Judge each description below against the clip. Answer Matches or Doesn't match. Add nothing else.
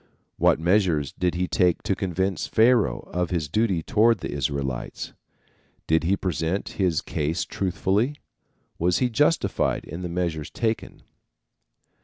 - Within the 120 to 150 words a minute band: Matches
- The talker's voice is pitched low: Matches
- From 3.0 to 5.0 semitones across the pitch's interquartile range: Matches